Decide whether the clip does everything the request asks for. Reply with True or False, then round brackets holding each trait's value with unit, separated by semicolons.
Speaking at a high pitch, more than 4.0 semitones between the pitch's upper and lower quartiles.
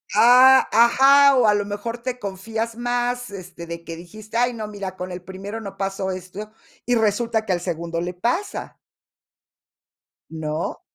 True (210 Hz; 4.4 semitones)